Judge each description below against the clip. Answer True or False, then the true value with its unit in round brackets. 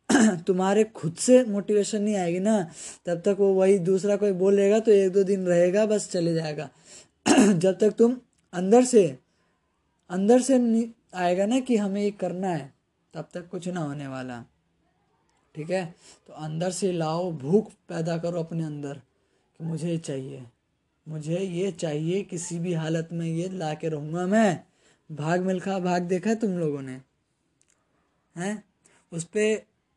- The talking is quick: False (160 wpm)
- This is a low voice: False (180 Hz)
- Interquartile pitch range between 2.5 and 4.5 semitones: True (4.0 semitones)